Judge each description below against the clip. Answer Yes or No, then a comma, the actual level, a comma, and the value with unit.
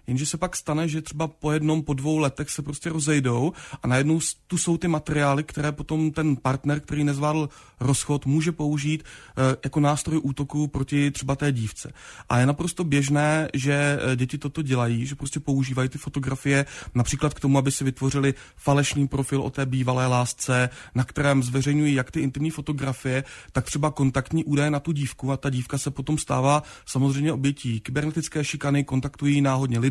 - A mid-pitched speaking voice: Yes, medium, 145 Hz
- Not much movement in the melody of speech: Yes, narrow, 2.0 semitones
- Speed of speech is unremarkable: No, fast, 175 wpm